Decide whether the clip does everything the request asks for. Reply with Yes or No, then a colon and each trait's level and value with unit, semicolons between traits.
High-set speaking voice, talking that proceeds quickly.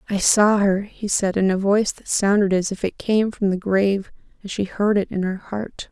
Yes: high, 200 Hz; fast, 245 wpm